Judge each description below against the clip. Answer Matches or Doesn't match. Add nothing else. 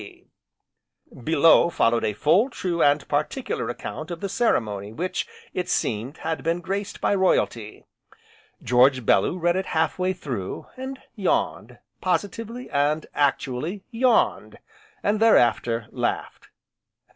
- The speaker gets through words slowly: Matches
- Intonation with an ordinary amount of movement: Doesn't match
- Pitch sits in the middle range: Matches